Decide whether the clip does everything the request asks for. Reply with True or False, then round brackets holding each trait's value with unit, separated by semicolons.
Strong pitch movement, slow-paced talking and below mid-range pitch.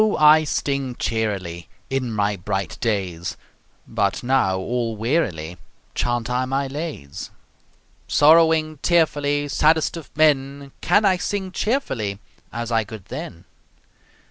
True (6.6 semitones; 115 wpm; 130 Hz)